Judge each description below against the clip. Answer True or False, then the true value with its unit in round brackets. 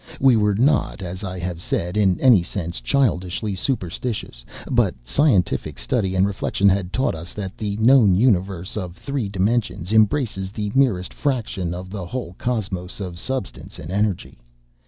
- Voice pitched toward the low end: True (100 Hz)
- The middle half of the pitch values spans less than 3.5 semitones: False (4.1 semitones)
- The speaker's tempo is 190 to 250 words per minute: False (155 wpm)